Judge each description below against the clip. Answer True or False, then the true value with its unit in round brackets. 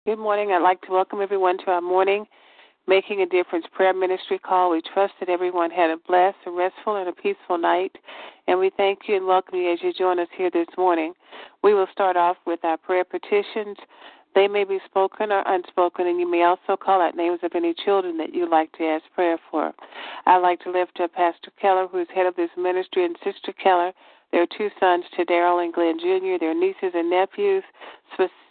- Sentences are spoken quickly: True (215 wpm)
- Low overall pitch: False (185 Hz)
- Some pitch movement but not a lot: False (1.8 semitones)